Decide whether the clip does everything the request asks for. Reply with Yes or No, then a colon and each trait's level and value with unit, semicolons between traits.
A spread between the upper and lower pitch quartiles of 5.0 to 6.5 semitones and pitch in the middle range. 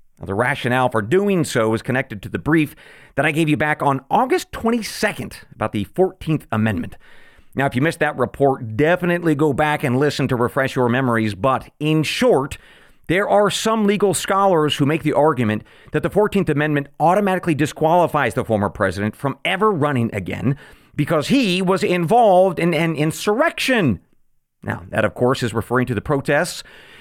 Yes: wide, 5.6 semitones; medium, 145 Hz